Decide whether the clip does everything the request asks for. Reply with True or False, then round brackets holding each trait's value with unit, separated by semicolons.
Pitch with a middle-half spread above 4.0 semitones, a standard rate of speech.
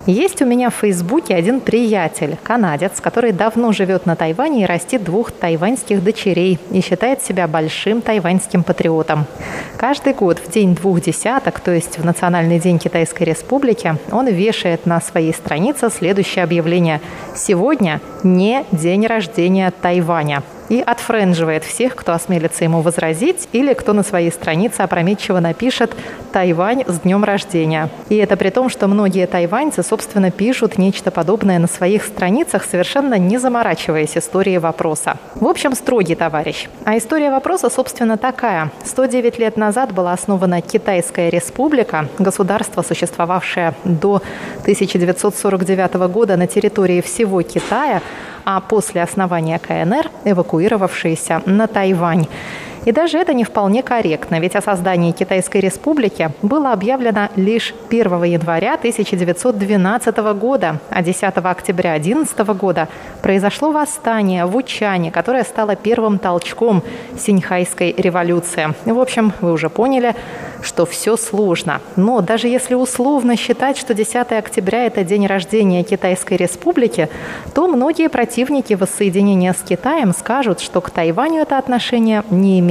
True (4.7 semitones; 135 wpm)